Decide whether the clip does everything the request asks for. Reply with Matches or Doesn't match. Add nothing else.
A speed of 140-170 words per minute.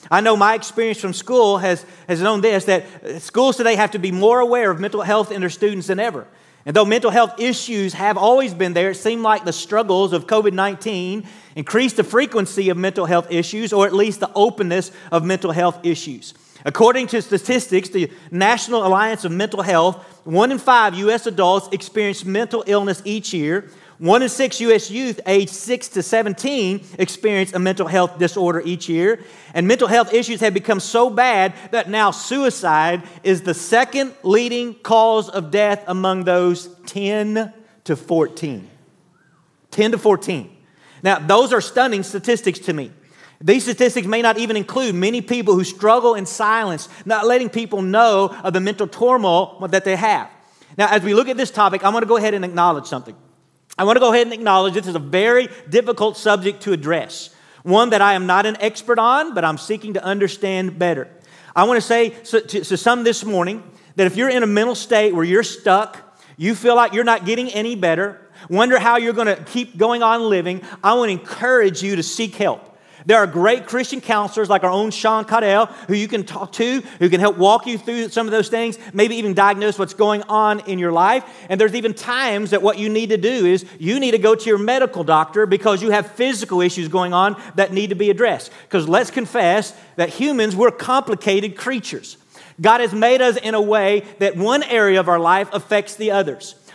Doesn't match